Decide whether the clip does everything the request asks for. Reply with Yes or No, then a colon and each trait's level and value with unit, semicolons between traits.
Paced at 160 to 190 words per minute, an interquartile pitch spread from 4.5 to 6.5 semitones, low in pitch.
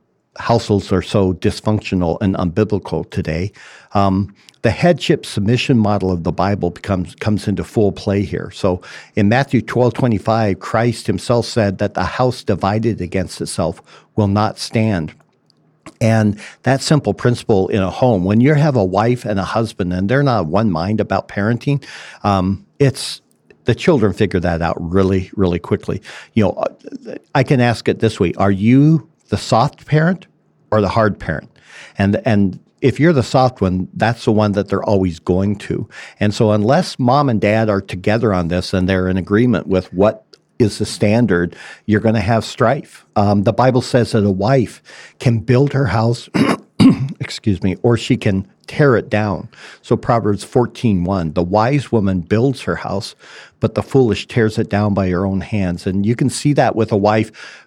No: average, 180 wpm; average, 3.7 semitones; low, 105 Hz